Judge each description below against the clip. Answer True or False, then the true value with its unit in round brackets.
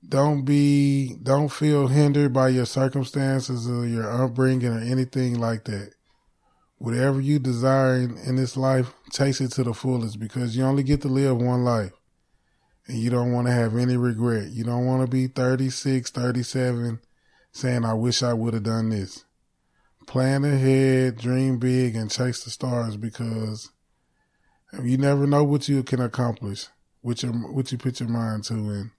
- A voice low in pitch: True (125 Hz)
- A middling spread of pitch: False (2.2 semitones)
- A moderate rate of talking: True (170 wpm)